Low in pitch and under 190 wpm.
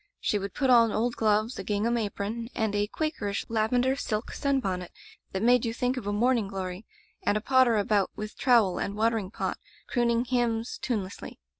No: high, 225 Hz; average, 180 wpm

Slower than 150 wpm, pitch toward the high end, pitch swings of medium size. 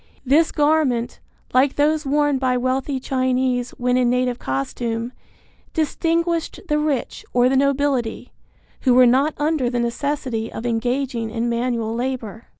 Yes: average, 140 wpm; very high, 255 Hz; average, 3.0 semitones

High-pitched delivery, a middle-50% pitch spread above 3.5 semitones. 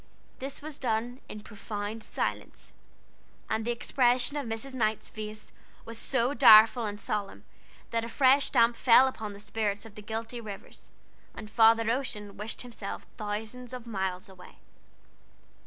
No: high, 225 Hz; narrow, 2.6 semitones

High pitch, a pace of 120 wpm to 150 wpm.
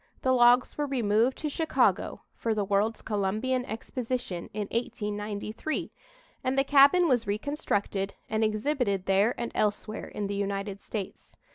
Yes: high, 220 Hz; average, 140 wpm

